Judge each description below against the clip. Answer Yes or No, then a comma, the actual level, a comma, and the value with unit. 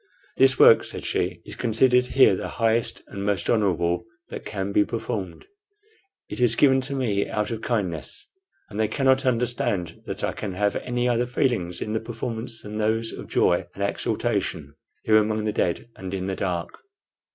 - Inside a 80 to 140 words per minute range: No, average, 180 wpm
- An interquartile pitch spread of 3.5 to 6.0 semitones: Yes, average, 3.9 semitones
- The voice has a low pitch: Yes, low, 110 Hz